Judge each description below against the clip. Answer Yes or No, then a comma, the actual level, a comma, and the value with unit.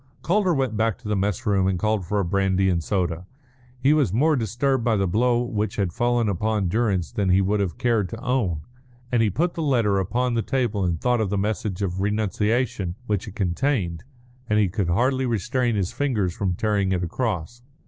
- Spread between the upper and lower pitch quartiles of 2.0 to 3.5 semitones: No, average, 4.3 semitones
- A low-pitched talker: Yes, low, 105 Hz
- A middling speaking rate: No, fast, 210 wpm